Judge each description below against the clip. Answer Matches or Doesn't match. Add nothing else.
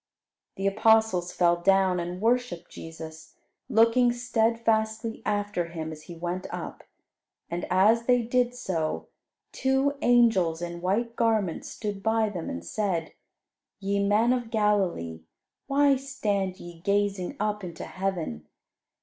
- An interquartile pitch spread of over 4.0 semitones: Matches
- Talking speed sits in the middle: Doesn't match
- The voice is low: Doesn't match